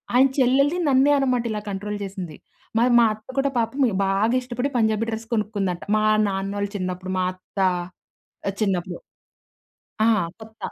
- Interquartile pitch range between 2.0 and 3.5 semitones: No, average, 4.2 semitones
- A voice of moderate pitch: No, high, 215 Hz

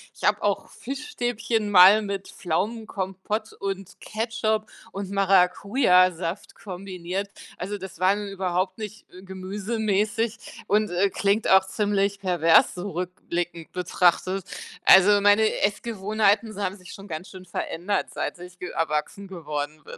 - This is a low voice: No, high, 195 Hz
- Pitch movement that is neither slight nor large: No, narrow, 2.3 semitones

